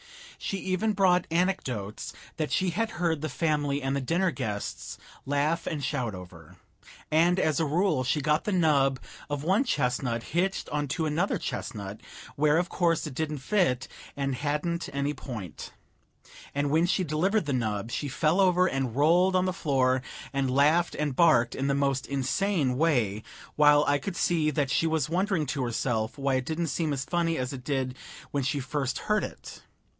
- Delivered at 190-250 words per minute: No, average, 180 wpm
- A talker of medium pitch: Yes, medium, 150 Hz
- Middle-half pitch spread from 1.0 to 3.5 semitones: No, average, 4.4 semitones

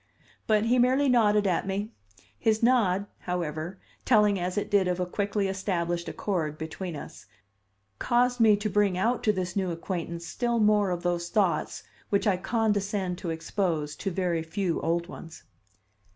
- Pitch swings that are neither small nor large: Yes, average, 3.4 semitones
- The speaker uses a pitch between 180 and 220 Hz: Yes, high, 190 Hz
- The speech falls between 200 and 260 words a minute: No, average, 165 wpm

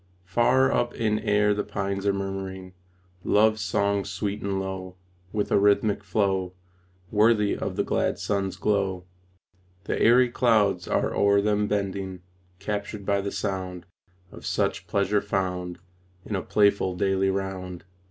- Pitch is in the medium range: No, low, 100 Hz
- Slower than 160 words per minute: Yes, average, 145 wpm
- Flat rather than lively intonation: Yes, narrow, 1.5 semitones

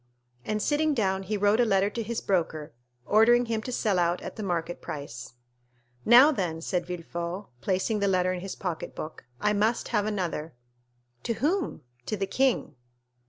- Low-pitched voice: No, high, 195 Hz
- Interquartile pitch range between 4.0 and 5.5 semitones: Yes, average, 4.3 semitones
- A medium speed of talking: Yes, average, 170 wpm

